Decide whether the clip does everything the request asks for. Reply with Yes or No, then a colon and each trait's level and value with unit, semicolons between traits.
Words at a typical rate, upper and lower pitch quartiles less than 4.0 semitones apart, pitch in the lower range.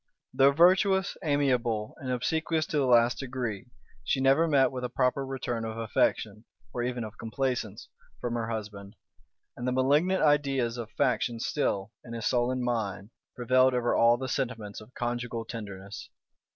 Yes: average, 160 wpm; average, 2.8 semitones; low, 125 Hz